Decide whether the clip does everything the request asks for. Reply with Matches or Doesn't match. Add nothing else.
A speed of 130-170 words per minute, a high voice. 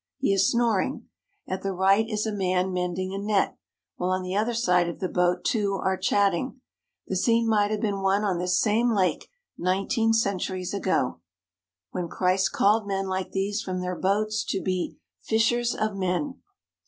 Doesn't match